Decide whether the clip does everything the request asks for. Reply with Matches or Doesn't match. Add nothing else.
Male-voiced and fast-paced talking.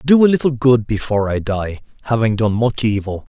Matches